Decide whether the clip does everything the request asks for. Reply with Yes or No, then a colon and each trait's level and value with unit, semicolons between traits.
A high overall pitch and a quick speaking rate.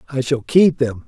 No: low, 135 Hz; fast, 225 wpm